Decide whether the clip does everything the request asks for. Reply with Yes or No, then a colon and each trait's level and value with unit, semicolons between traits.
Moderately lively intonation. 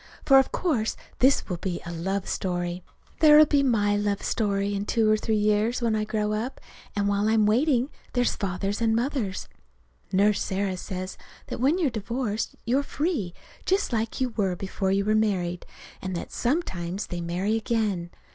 Yes: average, 3.8 semitones